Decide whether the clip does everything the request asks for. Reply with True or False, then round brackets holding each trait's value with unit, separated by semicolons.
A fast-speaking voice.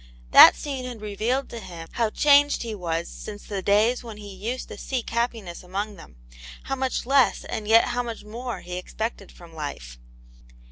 False (185 wpm)